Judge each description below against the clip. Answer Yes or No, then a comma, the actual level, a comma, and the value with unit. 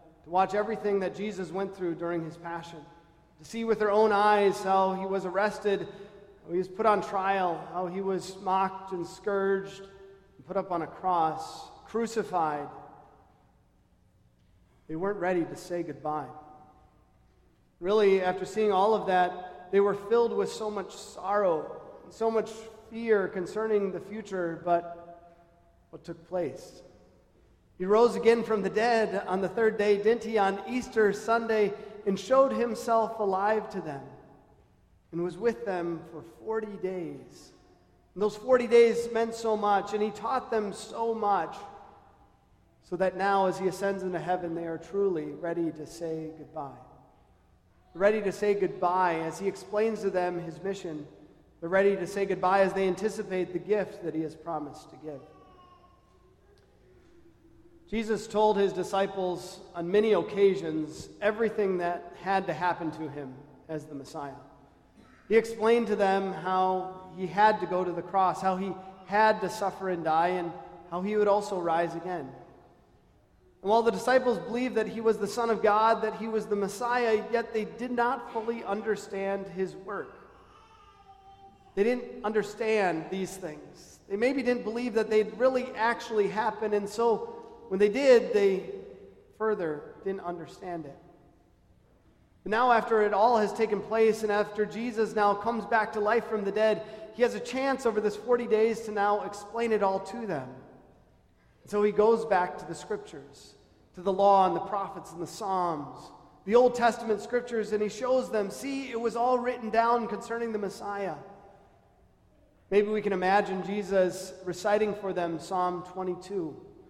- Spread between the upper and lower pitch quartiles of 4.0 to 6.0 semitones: No, average, 3.4 semitones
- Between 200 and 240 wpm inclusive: No, average, 165 wpm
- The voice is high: Yes, high, 200 Hz